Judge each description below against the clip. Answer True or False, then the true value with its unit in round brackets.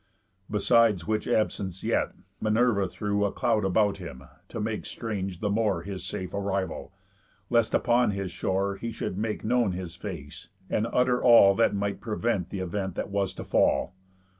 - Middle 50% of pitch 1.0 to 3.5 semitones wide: True (2.6 semitones)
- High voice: False (100 Hz)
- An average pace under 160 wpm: False (165 wpm)